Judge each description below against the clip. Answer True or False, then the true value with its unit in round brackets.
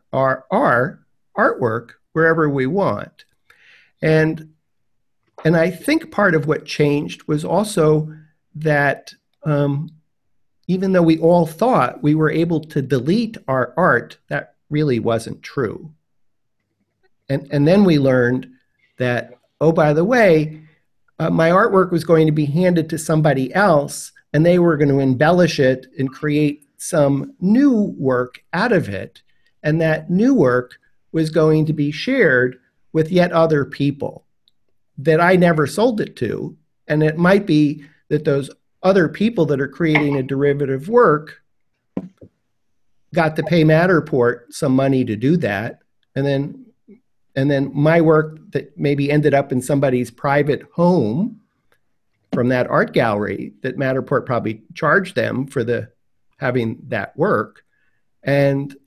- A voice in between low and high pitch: True (150 Hz)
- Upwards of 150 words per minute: False (145 wpm)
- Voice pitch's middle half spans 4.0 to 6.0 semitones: False (3.5 semitones)